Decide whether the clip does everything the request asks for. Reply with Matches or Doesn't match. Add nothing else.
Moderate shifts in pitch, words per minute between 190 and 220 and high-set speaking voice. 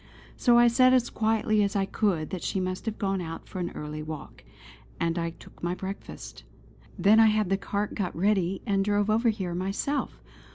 Matches